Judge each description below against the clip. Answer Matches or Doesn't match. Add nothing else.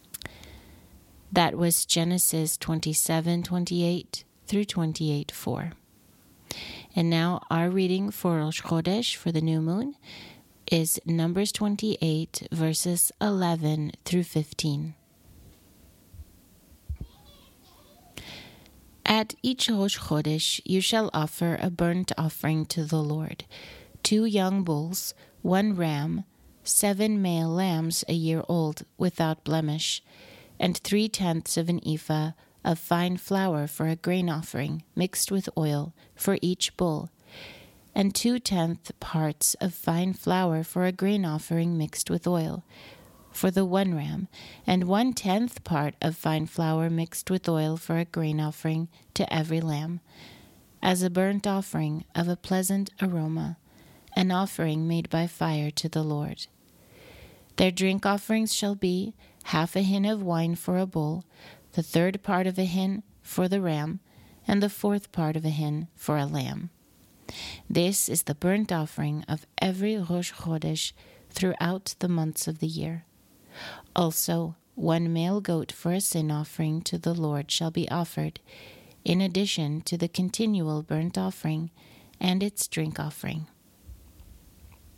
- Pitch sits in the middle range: Matches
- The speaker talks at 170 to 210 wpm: Doesn't match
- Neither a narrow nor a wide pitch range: Matches